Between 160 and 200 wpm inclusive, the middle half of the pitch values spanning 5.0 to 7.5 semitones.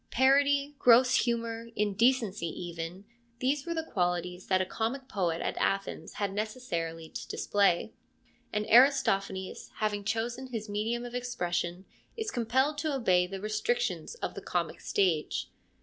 No: average, 145 wpm; average, 5.3 semitones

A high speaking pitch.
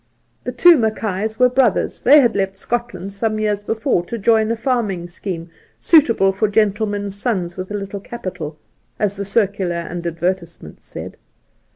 Yes: high, 205 Hz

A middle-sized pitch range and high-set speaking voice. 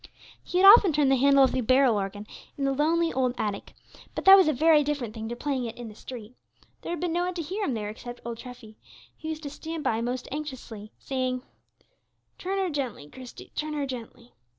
Yes: average, 4.6 semitones; very high, 265 Hz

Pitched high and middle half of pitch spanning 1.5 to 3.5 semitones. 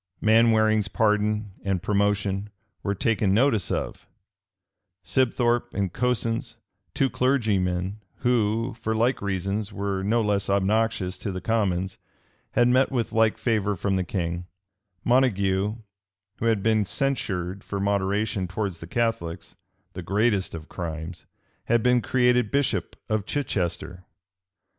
No: low, 105 Hz; average, 3.2 semitones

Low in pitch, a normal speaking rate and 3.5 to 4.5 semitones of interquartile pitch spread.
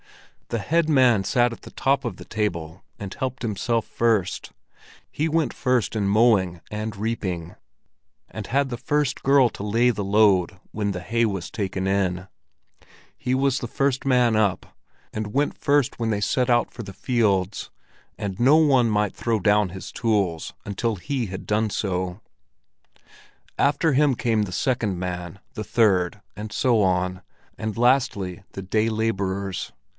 Yes: low, 110 Hz; average, 160 wpm; average, 4.2 semitones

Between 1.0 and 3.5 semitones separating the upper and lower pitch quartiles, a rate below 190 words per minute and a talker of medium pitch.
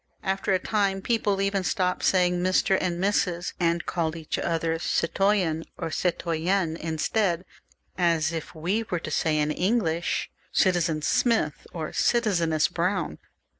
Yes: average, 2.9 semitones; average, 140 wpm; medium, 175 Hz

